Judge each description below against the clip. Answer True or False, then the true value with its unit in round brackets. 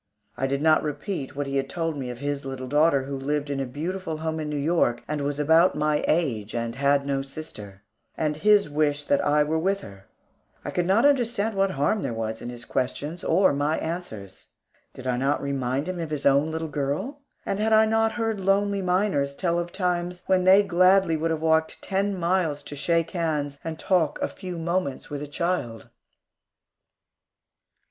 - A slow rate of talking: False (200 wpm)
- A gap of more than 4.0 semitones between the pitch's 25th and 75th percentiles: True (4.5 semitones)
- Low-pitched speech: False (155 Hz)